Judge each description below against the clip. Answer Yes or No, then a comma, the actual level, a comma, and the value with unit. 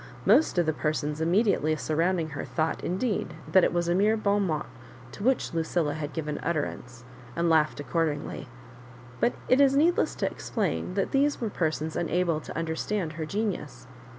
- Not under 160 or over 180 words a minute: Yes, average, 175 wpm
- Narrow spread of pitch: No, average, 4.6 semitones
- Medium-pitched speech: Yes, medium, 170 Hz